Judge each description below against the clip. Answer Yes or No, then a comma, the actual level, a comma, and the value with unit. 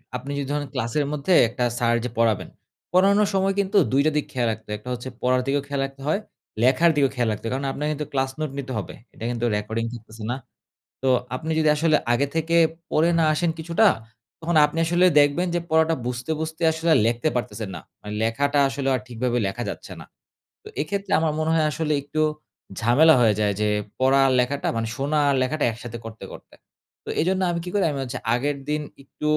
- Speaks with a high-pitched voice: No, medium, 140 Hz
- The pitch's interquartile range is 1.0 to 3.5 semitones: No, average, 4.6 semitones